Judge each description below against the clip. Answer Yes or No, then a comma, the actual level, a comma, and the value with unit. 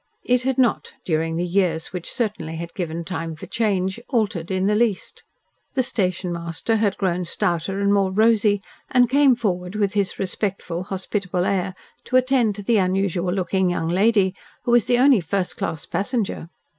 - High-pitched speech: Yes, high, 195 Hz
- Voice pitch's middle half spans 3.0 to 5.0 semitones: Yes, average, 3.7 semitones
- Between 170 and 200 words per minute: Yes, average, 175 wpm